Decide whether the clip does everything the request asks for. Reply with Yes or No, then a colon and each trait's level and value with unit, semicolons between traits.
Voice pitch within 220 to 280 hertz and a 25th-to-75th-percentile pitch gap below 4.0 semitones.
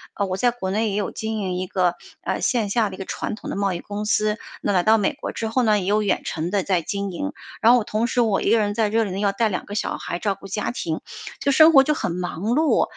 No: high, 210 Hz; average, 2.8 semitones